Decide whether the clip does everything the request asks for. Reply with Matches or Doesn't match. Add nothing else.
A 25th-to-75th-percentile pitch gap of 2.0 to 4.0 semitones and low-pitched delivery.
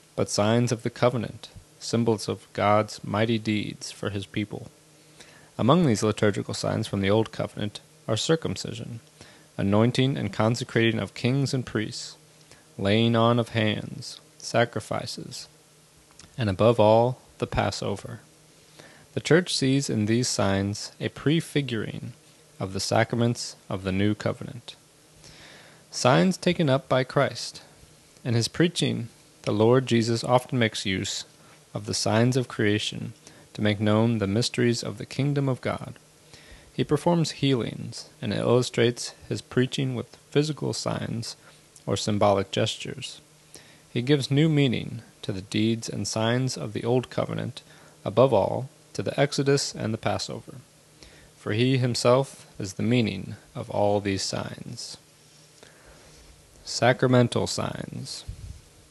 Doesn't match